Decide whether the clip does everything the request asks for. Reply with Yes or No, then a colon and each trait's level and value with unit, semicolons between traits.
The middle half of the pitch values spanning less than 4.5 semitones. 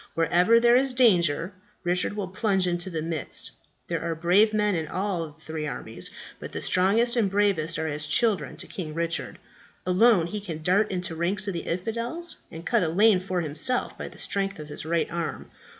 Yes: average, 4.1 semitones